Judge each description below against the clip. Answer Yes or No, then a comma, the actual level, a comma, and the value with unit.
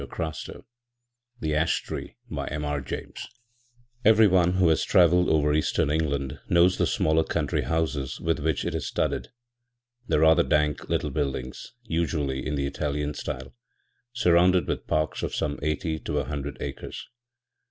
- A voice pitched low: Yes, very low, 75 Hz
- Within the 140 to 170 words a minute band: Yes, average, 150 wpm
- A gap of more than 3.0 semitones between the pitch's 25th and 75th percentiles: No, narrow, 2.6 semitones